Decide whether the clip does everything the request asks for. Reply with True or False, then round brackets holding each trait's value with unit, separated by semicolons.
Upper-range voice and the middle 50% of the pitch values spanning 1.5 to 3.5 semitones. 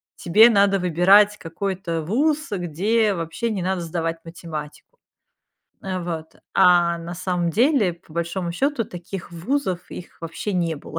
False (180 Hz; 3.2 semitones)